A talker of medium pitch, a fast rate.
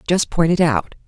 Yes: medium, 165 Hz; fast, 225 wpm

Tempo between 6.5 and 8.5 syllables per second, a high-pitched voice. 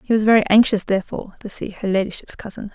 Yes: 6.9 syllables/s; high, 205 Hz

